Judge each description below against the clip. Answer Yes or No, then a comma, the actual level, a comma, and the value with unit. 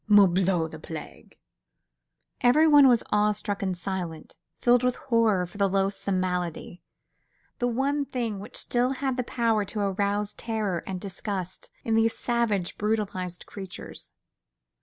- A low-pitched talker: No, high, 205 Hz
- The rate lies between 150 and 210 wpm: No, average, 140 wpm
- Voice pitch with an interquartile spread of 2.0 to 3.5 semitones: No, average, 4.1 semitones